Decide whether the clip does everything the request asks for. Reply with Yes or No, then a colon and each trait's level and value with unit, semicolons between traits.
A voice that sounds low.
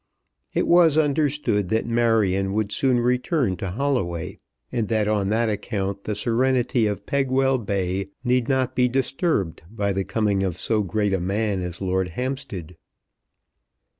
Yes: low, 110 Hz